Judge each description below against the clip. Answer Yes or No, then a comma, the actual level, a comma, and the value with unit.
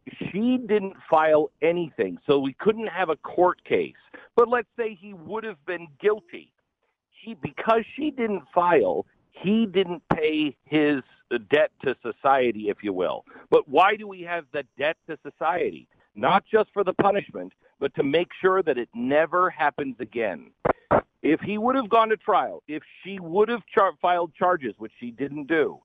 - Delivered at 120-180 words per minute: Yes, average, 175 wpm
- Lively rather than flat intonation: Yes, wide, 6.4 semitones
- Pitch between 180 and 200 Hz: Yes, medium, 185 Hz